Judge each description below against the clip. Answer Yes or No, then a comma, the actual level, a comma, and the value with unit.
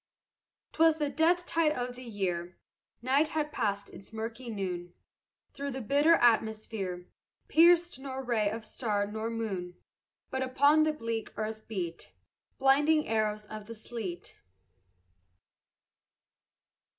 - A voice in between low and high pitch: No, high, 230 Hz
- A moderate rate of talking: No, slow, 125 wpm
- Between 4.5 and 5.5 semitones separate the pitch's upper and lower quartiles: Yes, average, 5.1 semitones